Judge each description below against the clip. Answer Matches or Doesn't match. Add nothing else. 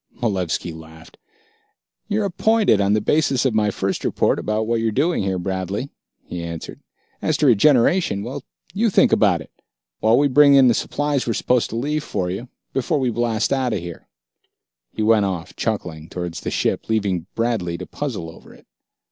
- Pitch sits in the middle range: Doesn't match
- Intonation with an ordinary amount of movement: Doesn't match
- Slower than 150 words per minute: Doesn't match